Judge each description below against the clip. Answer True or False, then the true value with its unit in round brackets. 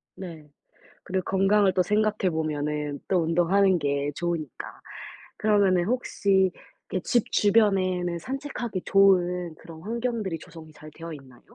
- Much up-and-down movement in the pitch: False (3.8 semitones)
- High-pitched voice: False (180 Hz)